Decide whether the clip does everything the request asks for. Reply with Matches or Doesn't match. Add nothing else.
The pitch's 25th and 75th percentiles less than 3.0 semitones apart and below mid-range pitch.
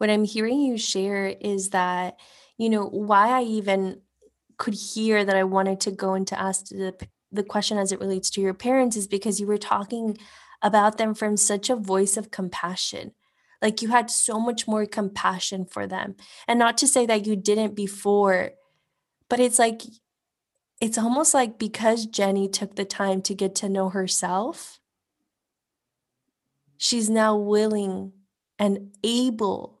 Doesn't match